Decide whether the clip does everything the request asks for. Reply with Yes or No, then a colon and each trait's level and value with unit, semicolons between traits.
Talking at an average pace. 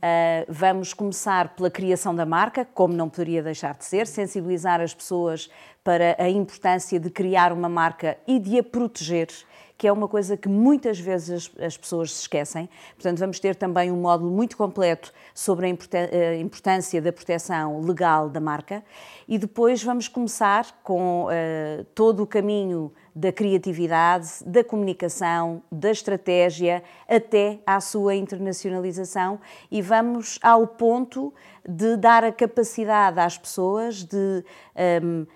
Yes: average, 145 wpm